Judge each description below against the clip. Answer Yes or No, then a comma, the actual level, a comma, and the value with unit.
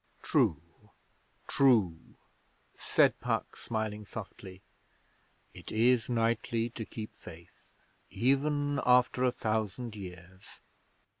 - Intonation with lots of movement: No, average, 3.7 semitones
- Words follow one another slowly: Yes, slow, 90 wpm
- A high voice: No, low, 110 Hz